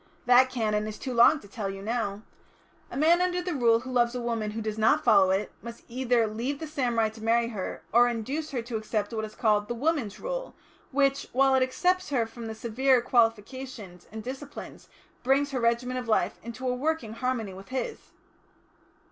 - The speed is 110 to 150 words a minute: No, average, 200 wpm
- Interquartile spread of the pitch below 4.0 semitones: Yes, average, 3.3 semitones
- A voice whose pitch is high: Yes, high, 240 Hz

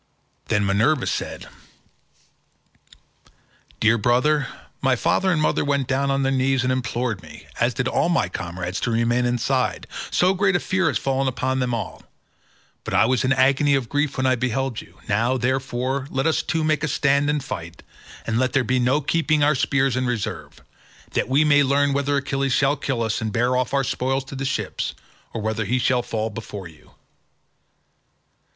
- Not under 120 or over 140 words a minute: No, average, 190 wpm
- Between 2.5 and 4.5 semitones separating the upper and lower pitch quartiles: Yes, average, 2.8 semitones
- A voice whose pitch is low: Yes, low, 130 Hz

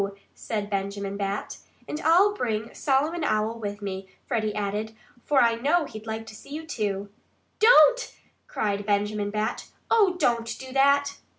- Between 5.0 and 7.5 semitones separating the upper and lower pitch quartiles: Yes, wide, 5.6 semitones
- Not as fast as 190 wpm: Yes, average, 155 wpm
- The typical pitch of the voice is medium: No, high, 225 Hz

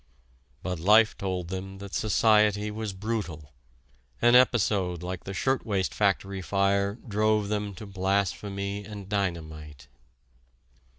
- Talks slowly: Yes, slow, 115 wpm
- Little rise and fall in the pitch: Yes, narrow, 2.2 semitones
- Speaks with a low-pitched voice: Yes, low, 100 Hz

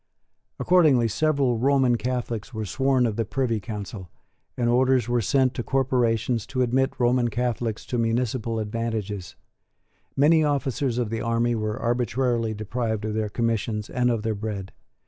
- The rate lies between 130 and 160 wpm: Yes, average, 150 wpm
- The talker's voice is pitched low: Yes, low, 120 Hz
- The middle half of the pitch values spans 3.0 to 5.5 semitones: No, narrow, 2.6 semitones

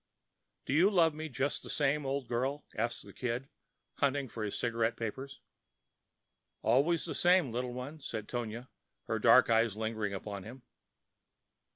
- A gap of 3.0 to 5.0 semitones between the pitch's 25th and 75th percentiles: Yes, average, 3.9 semitones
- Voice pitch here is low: Yes, low, 125 Hz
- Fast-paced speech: No, average, 155 wpm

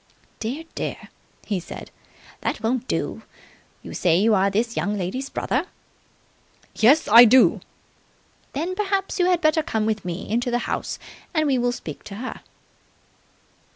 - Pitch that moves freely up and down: Yes, wide, 6.2 semitones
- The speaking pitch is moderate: No, high, 240 Hz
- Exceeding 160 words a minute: No, average, 155 wpm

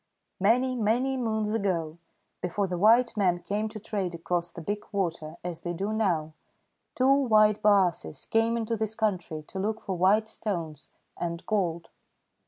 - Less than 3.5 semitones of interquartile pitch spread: No, average, 4.0 semitones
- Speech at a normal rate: Yes, average, 160 wpm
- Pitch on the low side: No, high, 200 Hz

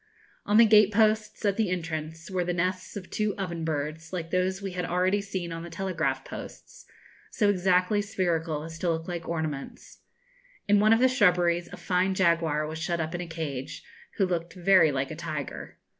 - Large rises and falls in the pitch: No, average, 3.0 semitones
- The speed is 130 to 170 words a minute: No, average, 195 wpm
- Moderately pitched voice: Yes, medium, 175 Hz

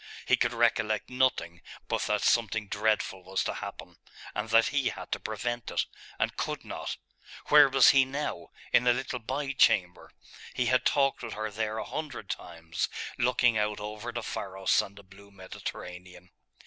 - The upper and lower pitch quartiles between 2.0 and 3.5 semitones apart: No, average, 4.3 semitones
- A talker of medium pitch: No, low, 110 Hz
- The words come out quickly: No, average, 175 wpm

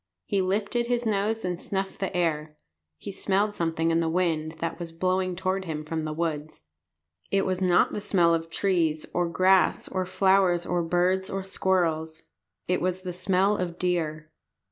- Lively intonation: No, narrow, 2.6 semitones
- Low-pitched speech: No, medium, 180 Hz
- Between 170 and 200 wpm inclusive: Yes, average, 175 wpm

